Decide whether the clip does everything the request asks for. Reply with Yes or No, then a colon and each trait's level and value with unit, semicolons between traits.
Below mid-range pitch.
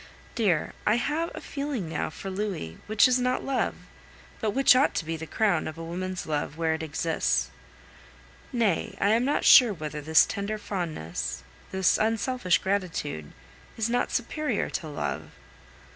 No: high, 190 Hz